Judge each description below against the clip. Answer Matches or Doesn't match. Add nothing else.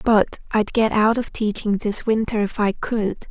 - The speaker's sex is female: Matches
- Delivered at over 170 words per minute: Matches